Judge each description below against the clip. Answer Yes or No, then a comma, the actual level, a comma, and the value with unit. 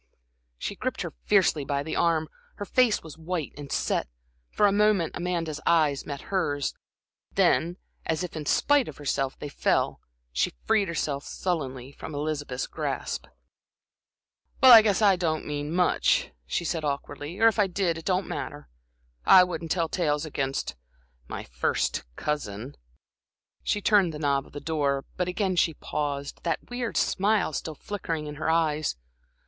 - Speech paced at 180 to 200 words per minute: No, average, 165 wpm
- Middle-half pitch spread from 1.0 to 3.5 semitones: No, average, 4.0 semitones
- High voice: No, medium, 160 Hz